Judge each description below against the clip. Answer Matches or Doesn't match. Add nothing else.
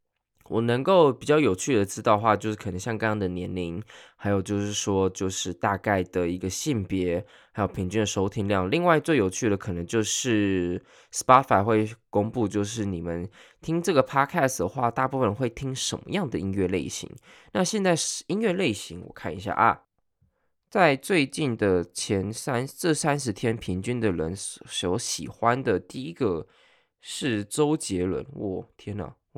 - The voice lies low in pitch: Matches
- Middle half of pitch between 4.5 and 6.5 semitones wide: Matches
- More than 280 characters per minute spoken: Doesn't match